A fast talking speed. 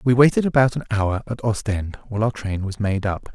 Yes: fast, 235 wpm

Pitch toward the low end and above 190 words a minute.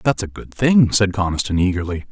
Yes: low, 100 Hz; average, 200 wpm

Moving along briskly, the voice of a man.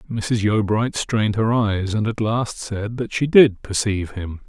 No: average, 190 wpm; male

